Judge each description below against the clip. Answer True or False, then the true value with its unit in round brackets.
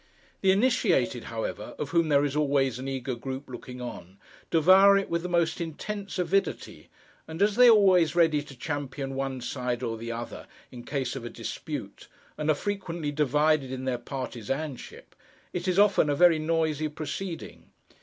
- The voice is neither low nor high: True (150 Hz)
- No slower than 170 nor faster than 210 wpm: True (175 wpm)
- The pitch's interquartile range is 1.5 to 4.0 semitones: False (5.0 semitones)